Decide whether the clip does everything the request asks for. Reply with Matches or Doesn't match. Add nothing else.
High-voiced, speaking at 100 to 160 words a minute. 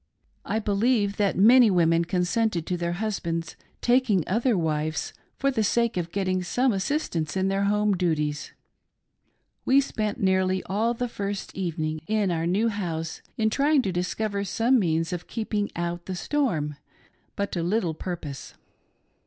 Matches